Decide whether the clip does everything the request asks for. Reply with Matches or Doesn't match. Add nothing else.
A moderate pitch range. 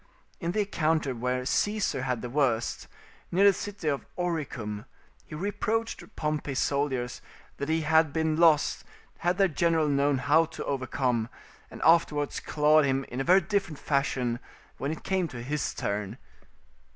Matches